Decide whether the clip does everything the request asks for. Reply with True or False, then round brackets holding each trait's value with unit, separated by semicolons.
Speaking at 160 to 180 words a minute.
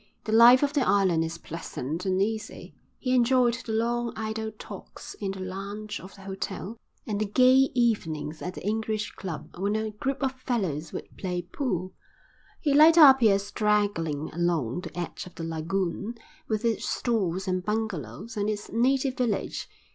True (170 wpm)